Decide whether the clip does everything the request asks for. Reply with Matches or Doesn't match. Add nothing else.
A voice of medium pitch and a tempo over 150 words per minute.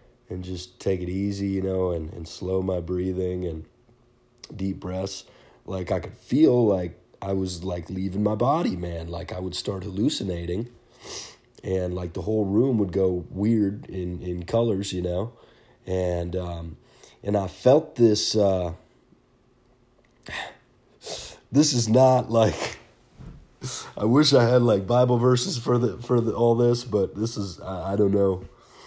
Doesn't match